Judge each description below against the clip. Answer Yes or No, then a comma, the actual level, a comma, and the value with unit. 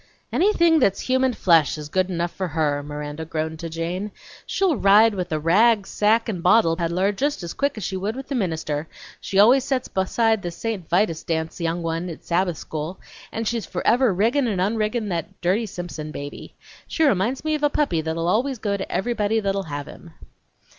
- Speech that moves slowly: No, average, 195 wpm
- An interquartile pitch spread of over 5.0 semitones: Yes, wide, 5.4 semitones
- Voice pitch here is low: No, high, 190 Hz